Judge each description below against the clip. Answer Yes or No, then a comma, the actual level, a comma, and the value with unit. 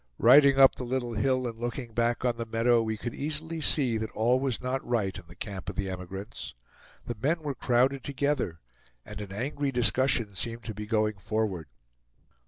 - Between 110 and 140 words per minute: No, average, 190 wpm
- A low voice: Yes, low, 120 Hz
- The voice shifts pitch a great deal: No, average, 3.8 semitones